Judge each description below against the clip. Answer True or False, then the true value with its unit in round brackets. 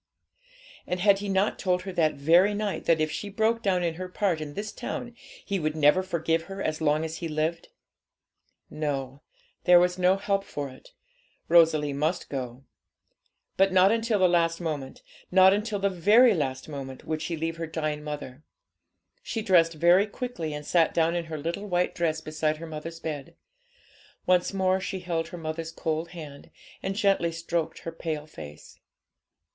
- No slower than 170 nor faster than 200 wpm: True (180 wpm)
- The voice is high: False (165 Hz)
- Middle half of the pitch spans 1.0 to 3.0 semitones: False (3.5 semitones)